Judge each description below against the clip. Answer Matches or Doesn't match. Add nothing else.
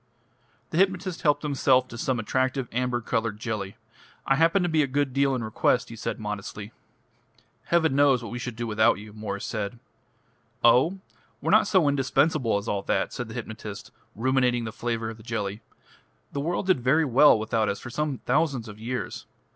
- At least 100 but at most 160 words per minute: Doesn't match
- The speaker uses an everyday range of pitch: Matches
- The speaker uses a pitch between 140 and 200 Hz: Doesn't match